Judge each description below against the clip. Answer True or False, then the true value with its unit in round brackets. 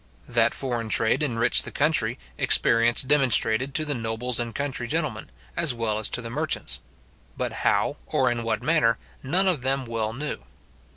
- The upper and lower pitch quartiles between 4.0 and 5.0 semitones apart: False (3.3 semitones)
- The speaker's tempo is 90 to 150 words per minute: False (170 wpm)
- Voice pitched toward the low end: True (120 Hz)